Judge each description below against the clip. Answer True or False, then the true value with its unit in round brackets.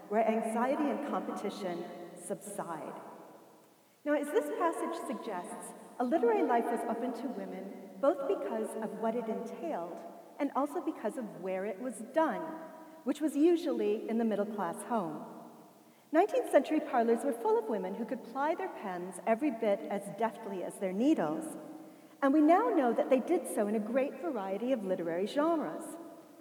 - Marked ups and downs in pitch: True (6.5 semitones)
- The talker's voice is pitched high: True (240 Hz)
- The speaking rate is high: False (165 wpm)